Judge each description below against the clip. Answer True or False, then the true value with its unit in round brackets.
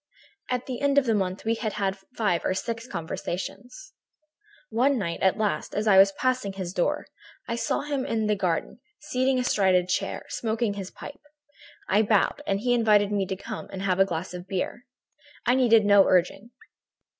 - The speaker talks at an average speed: True (195 wpm)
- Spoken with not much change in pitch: False (4.2 semitones)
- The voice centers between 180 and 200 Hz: False (210 Hz)